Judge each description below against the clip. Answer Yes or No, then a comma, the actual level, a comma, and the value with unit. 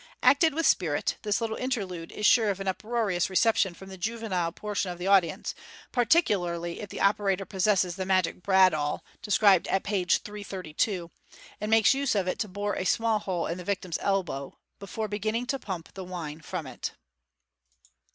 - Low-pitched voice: No, high, 195 Hz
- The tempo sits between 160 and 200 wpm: Yes, average, 175 wpm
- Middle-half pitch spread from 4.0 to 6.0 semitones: No, average, 3.0 semitones